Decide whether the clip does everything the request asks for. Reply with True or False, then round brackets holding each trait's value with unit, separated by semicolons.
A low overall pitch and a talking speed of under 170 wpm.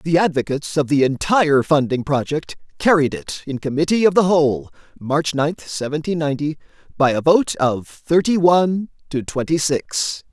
False (150 Hz; 155 wpm)